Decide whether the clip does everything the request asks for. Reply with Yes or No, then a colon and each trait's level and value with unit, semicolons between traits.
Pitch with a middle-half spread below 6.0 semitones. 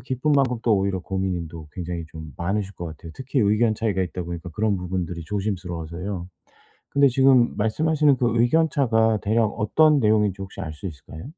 Yes: wide, 5.4 semitones